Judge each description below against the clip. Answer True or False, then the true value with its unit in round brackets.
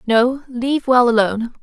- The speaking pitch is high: True (245 Hz)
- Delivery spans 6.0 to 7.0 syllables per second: False (5.0 syllables/s)